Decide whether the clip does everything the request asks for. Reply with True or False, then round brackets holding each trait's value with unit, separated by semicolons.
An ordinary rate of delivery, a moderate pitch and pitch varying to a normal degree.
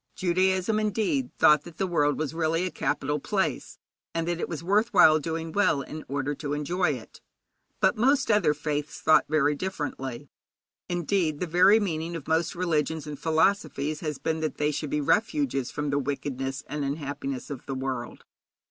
True (175 wpm; 155 Hz; 3.6 semitones)